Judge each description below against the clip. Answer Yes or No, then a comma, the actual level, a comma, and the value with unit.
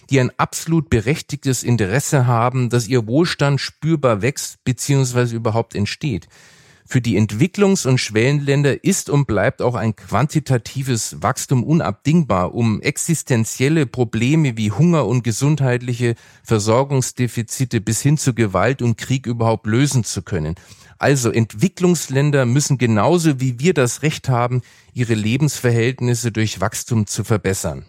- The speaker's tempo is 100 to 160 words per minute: Yes, average, 130 wpm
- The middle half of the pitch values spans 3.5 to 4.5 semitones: Yes, average, 3.8 semitones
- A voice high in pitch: No, low, 125 Hz